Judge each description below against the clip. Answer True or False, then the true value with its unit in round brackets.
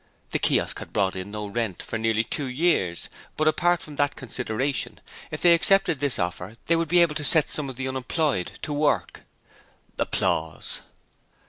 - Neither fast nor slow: True (180 wpm)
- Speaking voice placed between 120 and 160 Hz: True (135 Hz)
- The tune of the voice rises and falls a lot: True (6.4 semitones)